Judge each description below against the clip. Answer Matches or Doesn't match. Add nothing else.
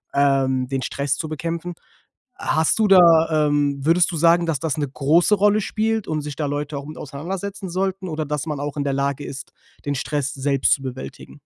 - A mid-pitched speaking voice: Matches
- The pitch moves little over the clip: Doesn't match